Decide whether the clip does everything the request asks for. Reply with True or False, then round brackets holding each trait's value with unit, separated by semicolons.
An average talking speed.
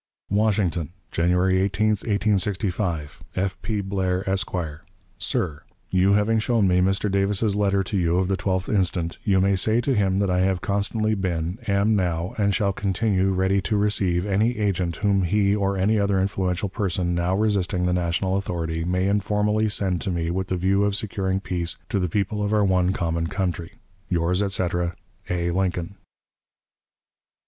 True (170 wpm)